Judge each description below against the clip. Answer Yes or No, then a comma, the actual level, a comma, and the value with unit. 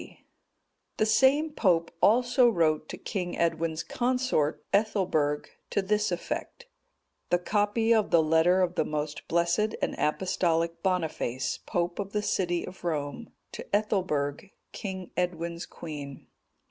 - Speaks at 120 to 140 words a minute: Yes, slow, 135 wpm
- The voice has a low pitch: No, medium, 175 Hz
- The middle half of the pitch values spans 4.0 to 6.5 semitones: Yes, average, 4.3 semitones